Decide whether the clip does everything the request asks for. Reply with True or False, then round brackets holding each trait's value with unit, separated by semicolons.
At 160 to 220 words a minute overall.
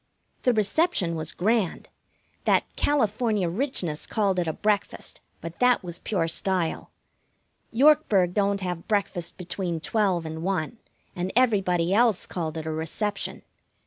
False (135 wpm)